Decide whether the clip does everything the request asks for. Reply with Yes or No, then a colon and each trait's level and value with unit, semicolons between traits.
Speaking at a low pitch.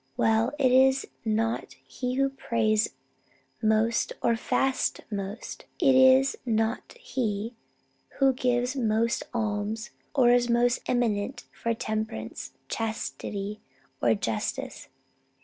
No: high, 230 Hz